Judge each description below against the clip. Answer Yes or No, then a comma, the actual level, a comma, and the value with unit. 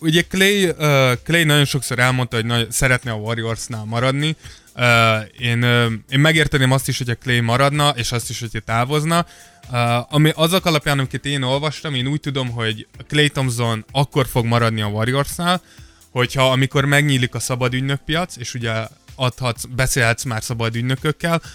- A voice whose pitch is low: Yes, low, 130 Hz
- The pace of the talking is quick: Yes, fast, 165 wpm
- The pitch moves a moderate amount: Yes, average, 3.5 semitones